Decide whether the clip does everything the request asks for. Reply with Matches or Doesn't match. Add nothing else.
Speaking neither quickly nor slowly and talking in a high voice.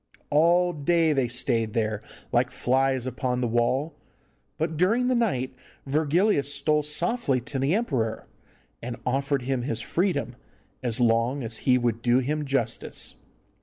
Doesn't match